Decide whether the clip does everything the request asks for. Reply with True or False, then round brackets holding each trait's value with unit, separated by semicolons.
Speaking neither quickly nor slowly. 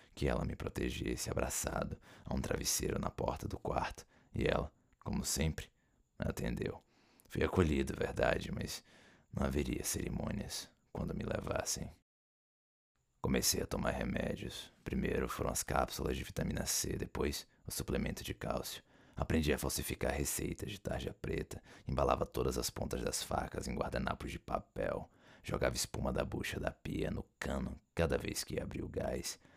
True (150 wpm)